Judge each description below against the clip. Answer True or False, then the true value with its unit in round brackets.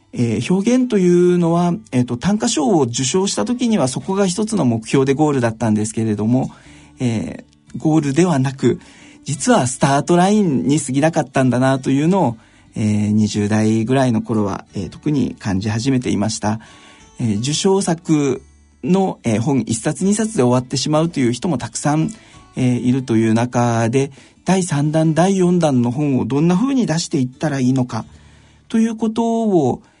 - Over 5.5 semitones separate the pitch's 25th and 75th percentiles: True (7.4 semitones)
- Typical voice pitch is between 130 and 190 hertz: True (135 Hz)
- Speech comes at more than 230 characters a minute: True (340 characters per minute)